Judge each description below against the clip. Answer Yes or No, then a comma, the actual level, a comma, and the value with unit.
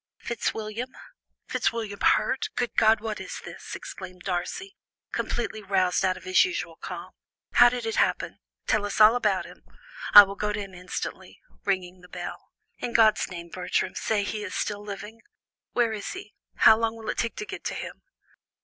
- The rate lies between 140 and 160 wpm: No, average, 180 wpm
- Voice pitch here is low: No, high, 210 Hz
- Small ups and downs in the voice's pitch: No, average, 3.5 semitones